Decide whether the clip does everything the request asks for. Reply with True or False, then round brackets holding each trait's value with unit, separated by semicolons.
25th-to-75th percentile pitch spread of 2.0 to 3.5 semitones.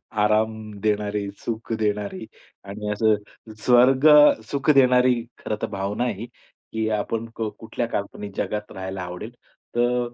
True (2.7 semitones)